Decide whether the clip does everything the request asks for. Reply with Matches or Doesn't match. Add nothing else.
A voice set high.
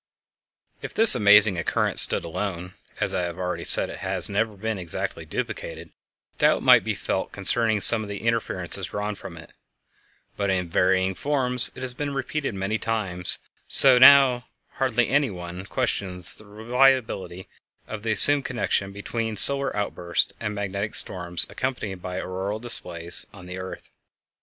Doesn't match